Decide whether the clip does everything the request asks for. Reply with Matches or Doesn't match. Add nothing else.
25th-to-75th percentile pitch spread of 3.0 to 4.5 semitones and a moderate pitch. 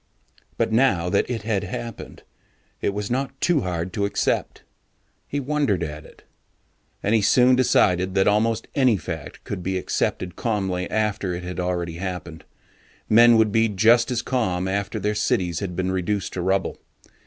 Doesn't match